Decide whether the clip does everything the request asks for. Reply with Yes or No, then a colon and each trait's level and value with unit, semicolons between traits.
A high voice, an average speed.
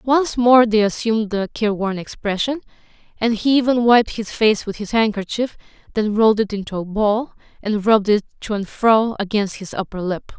Yes: high, 215 Hz; average, 185 wpm